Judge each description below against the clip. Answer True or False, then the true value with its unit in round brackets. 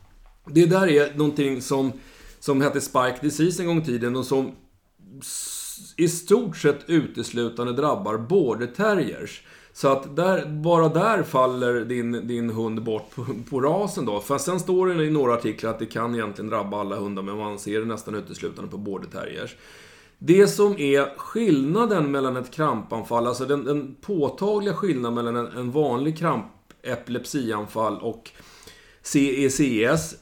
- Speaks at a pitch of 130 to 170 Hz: True (135 Hz)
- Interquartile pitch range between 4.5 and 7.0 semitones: True (5.4 semitones)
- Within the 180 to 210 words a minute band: False (155 wpm)